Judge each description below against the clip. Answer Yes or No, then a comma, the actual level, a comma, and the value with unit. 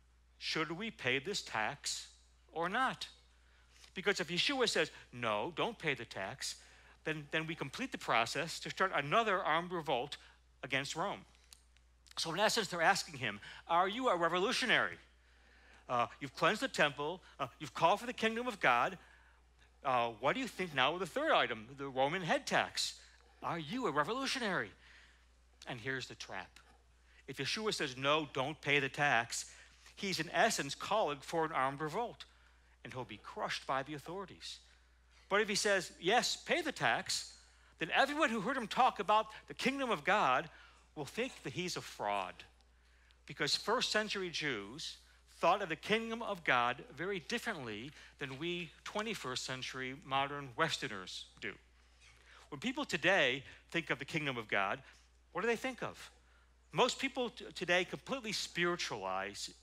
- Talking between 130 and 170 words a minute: Yes, average, 160 wpm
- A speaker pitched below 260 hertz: Yes, medium, 140 Hz